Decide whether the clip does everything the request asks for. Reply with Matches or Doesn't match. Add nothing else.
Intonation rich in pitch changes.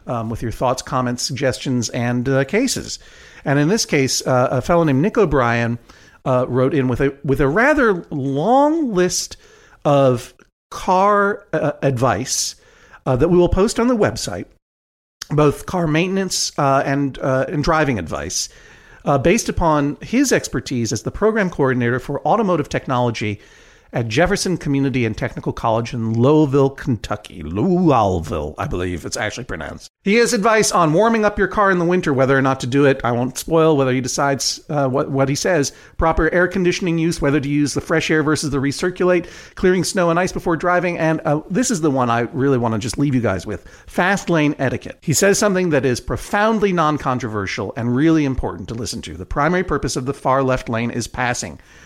Matches